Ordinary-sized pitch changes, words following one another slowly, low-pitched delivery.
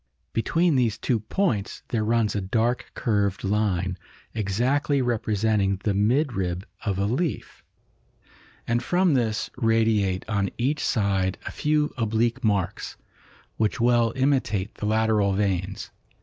Yes: average, 3.5 semitones; slow, 125 wpm; low, 110 Hz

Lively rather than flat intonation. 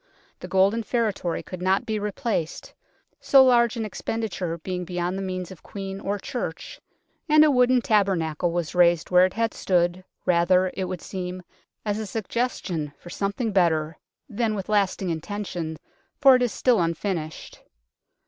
No: average, 3.9 semitones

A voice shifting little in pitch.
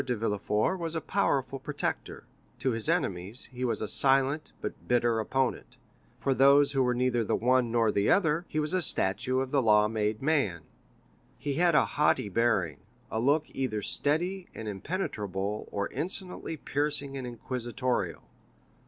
No: average, 4.9 semitones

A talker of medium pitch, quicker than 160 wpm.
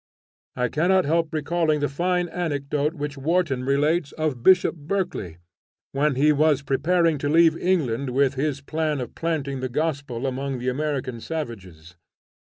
No: medium, 145 Hz; average, 150 wpm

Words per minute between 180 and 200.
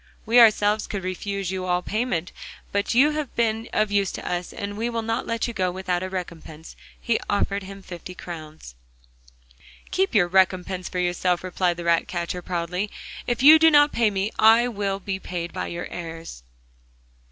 Yes: average, 185 wpm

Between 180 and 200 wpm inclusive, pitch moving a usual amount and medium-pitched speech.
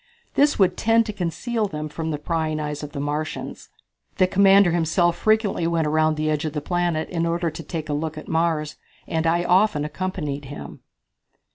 Yes: average, 190 wpm; average, 3.0 semitones; medium, 165 Hz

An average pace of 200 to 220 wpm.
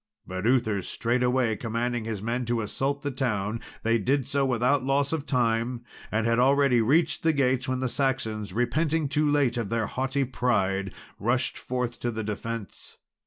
No: average, 170 wpm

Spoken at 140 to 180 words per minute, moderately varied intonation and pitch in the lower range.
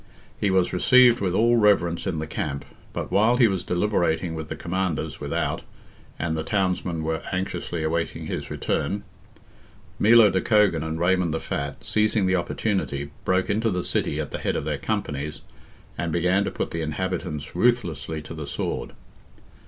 Yes: average, 170 wpm; average, 4.2 semitones; very low, 90 Hz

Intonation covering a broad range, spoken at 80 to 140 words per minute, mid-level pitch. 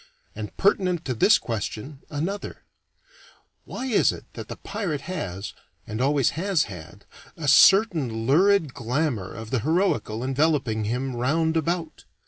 Yes: wide, 7.1 semitones; slow, 135 wpm; medium, 145 Hz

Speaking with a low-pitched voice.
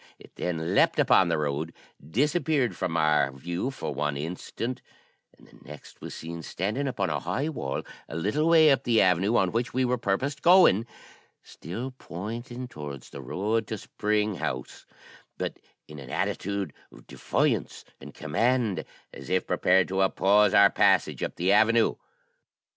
Yes: low, 100 Hz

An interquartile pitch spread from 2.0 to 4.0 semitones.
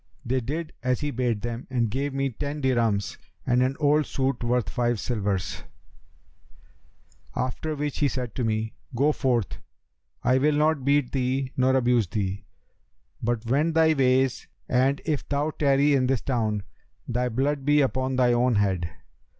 Yes: average, 2.9 semitones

